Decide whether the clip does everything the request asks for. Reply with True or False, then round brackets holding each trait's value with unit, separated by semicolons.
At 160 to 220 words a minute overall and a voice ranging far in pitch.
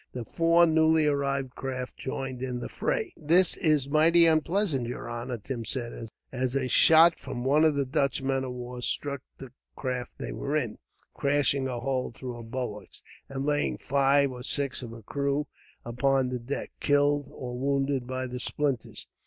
False (175 wpm; 2.5 semitones)